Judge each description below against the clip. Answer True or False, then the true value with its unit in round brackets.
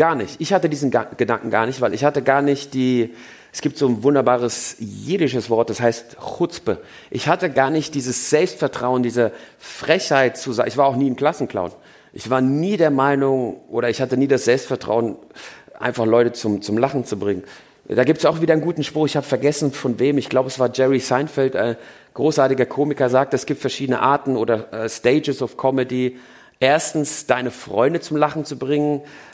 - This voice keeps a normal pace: False (200 wpm)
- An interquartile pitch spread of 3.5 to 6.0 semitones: False (3.0 semitones)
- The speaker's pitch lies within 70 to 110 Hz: False (135 Hz)